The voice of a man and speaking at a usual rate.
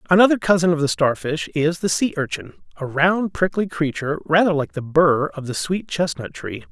Yes: male; average, 195 wpm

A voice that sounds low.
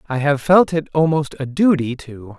No: medium, 145 Hz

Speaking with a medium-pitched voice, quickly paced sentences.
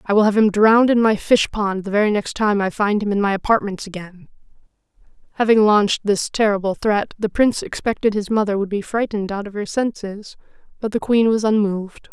No: high, 210 Hz; fast, 210 wpm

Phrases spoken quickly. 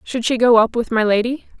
Yes: fast, 265 wpm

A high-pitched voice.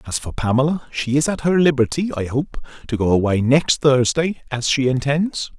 No: low, 135 Hz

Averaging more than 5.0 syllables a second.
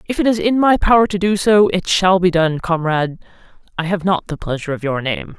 Yes: 5.9 syllables/s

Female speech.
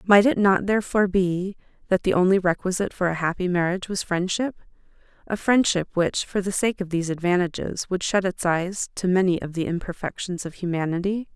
Yes: female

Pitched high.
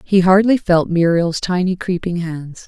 No: medium, 180 Hz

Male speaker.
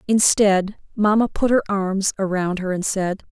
No: female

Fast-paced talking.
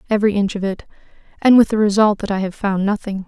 Yes: fast, 240 wpm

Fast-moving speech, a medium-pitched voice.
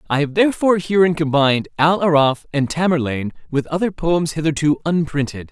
No: average, 150 wpm; medium, 155 Hz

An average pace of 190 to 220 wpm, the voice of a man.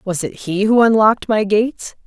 No: fast, 205 wpm; female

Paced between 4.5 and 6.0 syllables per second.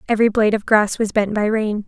No: 6.4 syllables/s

